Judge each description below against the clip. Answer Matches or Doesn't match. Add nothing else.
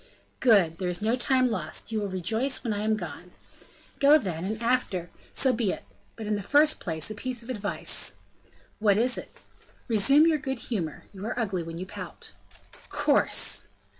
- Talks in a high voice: Matches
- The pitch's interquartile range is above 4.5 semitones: Matches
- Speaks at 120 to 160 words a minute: Doesn't match